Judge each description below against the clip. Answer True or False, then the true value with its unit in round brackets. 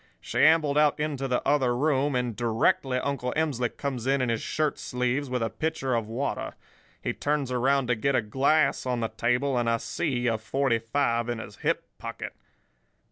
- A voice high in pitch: False (125 Hz)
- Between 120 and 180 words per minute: False (190 wpm)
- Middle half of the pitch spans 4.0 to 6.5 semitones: False (3.0 semitones)